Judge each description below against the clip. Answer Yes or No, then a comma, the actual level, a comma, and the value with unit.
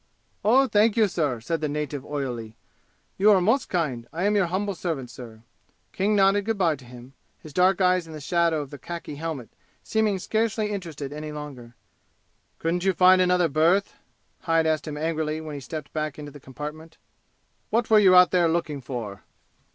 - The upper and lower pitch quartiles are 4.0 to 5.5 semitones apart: Yes, average, 4.5 semitones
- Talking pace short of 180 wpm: No, average, 190 wpm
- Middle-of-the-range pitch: Yes, medium, 165 Hz